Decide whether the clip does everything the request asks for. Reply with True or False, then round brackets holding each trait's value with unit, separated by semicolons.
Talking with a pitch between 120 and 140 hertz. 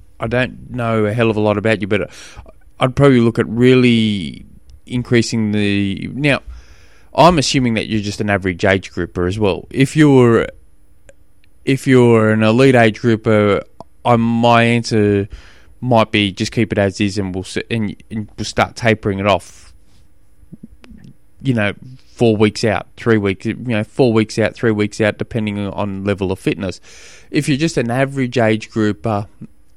False (110 Hz)